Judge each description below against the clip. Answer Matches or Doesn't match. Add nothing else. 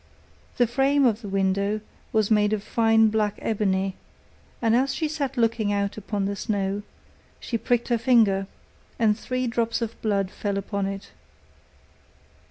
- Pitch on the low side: Doesn't match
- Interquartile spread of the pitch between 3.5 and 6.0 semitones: Doesn't match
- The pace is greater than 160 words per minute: Doesn't match